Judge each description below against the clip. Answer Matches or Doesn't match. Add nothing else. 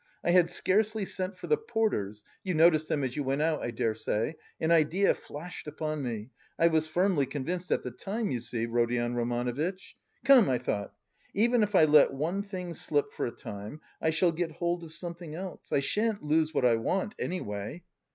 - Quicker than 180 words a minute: Matches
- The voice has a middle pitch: Matches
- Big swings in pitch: Matches